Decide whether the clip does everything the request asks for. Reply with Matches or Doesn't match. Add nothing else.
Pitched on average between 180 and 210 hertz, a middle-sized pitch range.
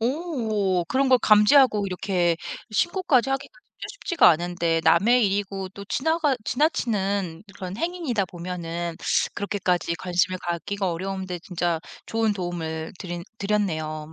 Matches